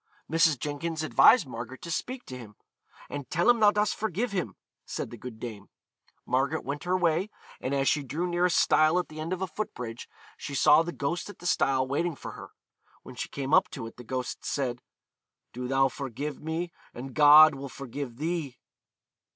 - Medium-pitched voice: Yes, medium, 145 Hz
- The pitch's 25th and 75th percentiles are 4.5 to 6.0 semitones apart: Yes, average, 4.8 semitones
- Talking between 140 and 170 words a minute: No, average, 200 wpm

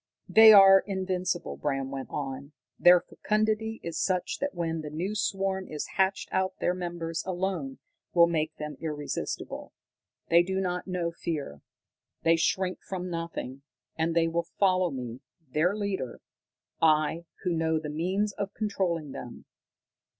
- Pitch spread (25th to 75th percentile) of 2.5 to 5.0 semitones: Yes, average, 3.5 semitones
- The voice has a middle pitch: Yes, medium, 170 Hz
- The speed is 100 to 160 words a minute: Yes, average, 145 wpm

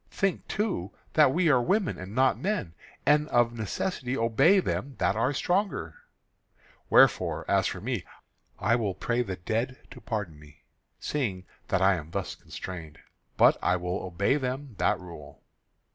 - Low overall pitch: Yes, low, 115 Hz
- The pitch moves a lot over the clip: Yes, wide, 7.8 semitones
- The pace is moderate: Yes, average, 160 wpm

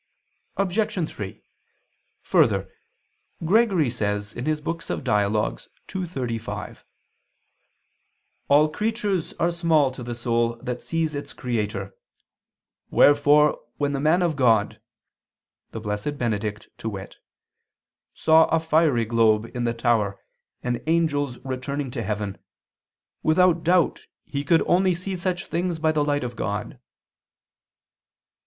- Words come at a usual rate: No, slow, 115 wpm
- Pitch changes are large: Yes, wide, 6.1 semitones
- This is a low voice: No, medium, 145 Hz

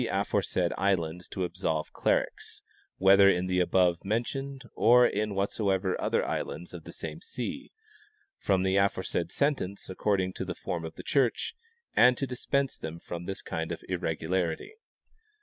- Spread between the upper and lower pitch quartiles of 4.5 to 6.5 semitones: No, average, 3.7 semitones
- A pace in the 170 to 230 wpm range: No, average, 155 wpm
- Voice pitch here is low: Yes, very low, 95 Hz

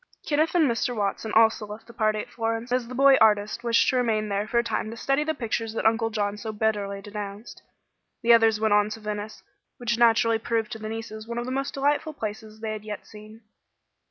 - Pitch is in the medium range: No, high, 225 Hz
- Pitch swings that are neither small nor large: No, narrow, 1.9 semitones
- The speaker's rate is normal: No, fast, 225 wpm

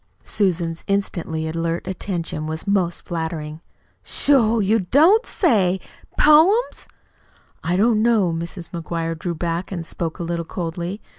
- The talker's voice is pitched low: No, medium, 175 Hz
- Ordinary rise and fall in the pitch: Yes, average, 4.0 semitones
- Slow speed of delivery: Yes, slow, 130 wpm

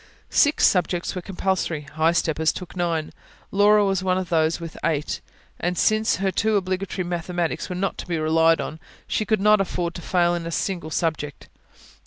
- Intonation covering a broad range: No, average, 2.8 semitones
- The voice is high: No, medium, 175 Hz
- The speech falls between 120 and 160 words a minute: No, average, 185 wpm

